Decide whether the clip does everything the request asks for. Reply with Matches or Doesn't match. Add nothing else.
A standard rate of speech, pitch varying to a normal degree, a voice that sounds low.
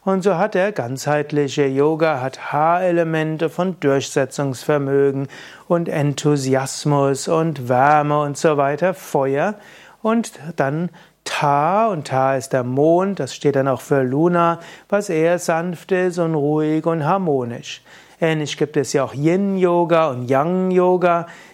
Doesn't match